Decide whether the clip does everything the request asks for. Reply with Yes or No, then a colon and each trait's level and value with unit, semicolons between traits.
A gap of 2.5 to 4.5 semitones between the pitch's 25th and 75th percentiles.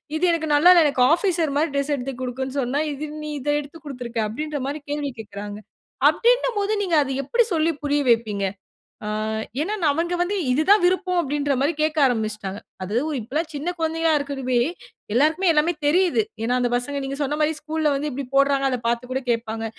Yes: average, 4.2 semitones